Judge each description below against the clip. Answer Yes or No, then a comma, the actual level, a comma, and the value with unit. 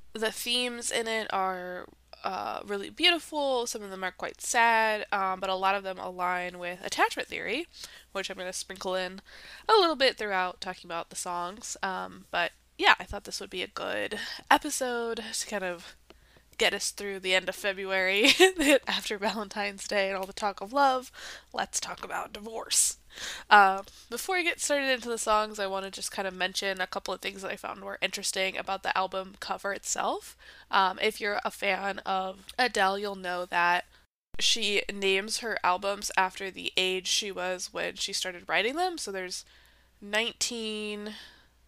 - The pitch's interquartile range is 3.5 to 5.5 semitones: No, average, 3.1 semitones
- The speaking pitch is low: No, high, 195 Hz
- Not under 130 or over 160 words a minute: No, average, 185 wpm